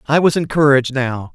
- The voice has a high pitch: No, medium, 140 Hz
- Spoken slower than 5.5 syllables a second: No, 5.7 syllables/s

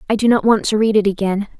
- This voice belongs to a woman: Yes, female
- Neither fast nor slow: No, fast, 300 wpm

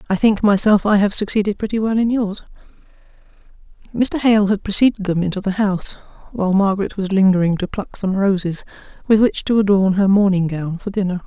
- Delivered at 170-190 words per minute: Yes, average, 185 wpm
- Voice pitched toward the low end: No, high, 200 Hz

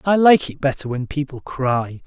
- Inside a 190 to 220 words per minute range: Yes, fast, 205 wpm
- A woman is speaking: No, male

